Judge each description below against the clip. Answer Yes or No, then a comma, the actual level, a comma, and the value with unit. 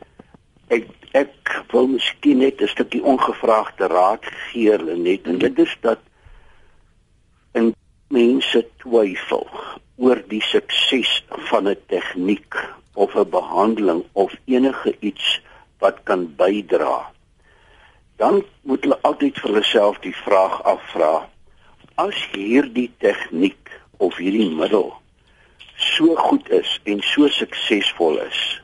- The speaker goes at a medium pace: No, slow, 120 wpm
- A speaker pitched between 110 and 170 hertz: Yes, low, 135 Hz